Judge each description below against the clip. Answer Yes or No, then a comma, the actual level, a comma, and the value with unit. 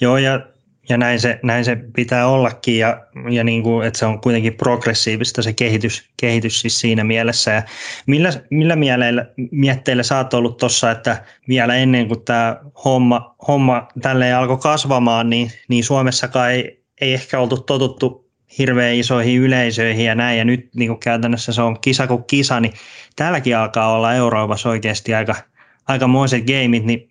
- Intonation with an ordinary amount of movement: No, narrow, 1.9 semitones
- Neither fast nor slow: No, fast, 165 wpm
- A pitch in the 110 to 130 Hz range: Yes, low, 120 Hz